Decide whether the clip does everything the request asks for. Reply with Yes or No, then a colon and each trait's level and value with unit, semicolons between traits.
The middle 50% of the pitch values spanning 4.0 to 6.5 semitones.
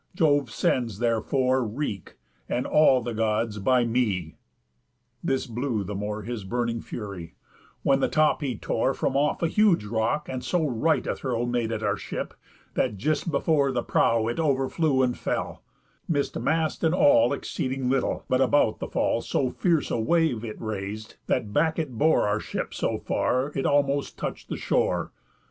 Yes: average, 4.5 semitones